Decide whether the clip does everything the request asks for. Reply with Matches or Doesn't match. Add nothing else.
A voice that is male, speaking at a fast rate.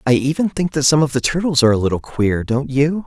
Matches